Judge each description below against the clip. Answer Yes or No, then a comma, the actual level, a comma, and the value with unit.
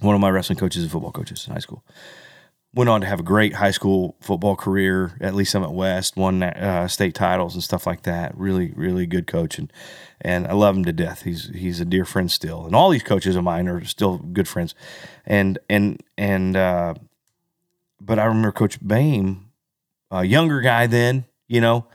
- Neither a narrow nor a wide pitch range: Yes, average, 3.6 semitones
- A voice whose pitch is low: Yes, very low, 95 Hz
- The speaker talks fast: Yes, fast, 210 wpm